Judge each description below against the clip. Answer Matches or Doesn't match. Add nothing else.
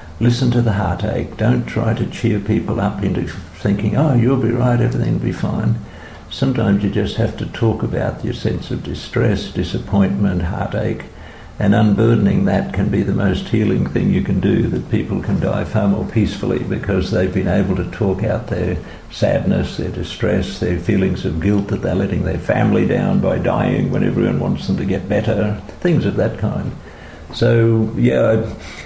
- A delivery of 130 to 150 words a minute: Doesn't match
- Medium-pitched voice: Doesn't match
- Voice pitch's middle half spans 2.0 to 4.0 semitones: Matches